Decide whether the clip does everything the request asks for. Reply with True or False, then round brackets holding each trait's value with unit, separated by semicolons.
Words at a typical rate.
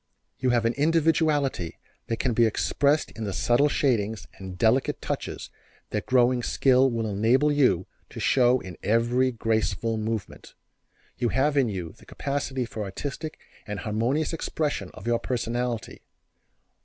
True (145 wpm)